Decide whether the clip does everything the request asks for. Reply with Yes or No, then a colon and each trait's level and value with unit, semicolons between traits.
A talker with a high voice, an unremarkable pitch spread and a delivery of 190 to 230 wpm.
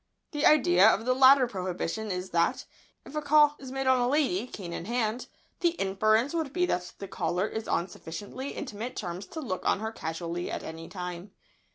No: high, 220 Hz; wide, 6.6 semitones; fast, 205 wpm